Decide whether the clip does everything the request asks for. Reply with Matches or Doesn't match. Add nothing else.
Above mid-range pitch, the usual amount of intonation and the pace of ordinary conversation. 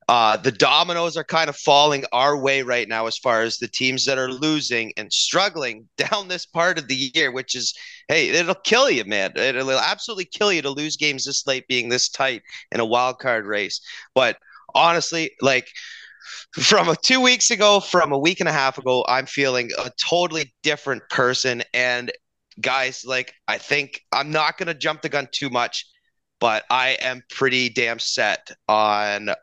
Doesn't match